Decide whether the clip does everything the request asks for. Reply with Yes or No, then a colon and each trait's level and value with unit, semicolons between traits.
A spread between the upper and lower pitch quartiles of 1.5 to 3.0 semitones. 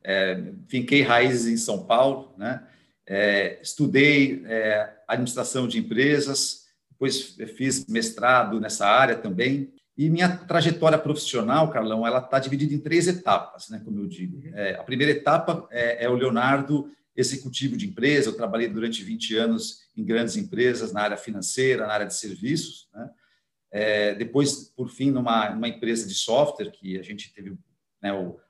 No: average, 4.8 semitones